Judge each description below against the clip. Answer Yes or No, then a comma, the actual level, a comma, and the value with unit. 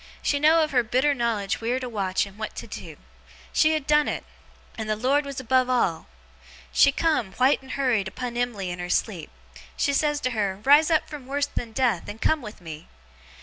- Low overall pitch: No, very high, 250 Hz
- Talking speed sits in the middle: No, fast, 215 wpm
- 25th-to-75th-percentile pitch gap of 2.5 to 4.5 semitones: No, average, 5.1 semitones